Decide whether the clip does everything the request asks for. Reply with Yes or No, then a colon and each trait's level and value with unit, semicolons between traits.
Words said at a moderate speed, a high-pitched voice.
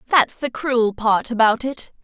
Yes: average, 175 wpm; high, 240 Hz